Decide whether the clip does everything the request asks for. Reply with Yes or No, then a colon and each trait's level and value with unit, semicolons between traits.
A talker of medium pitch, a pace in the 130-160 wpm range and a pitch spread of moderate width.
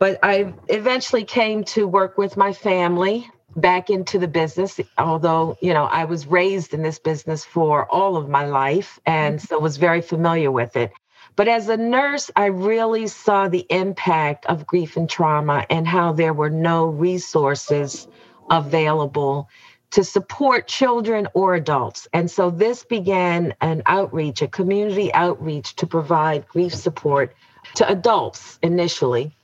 Yes: medium, 175 Hz; average, 155 wpm; average, 3.9 semitones